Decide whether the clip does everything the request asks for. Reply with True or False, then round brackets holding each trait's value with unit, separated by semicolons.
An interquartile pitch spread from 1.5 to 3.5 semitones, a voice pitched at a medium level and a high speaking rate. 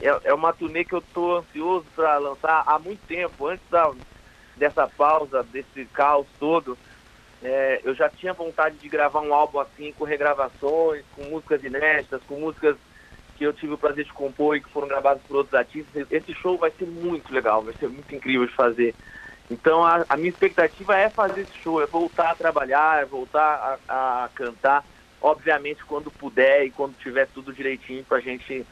True (3.2 semitones; 150 Hz; 190 wpm)